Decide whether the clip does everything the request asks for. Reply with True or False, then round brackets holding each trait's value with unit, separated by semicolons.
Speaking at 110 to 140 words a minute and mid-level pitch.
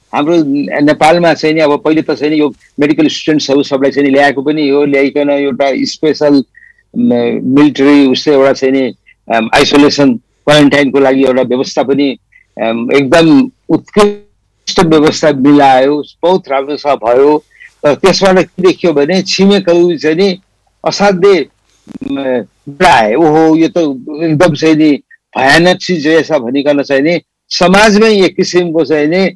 True (135 wpm; 150 Hz)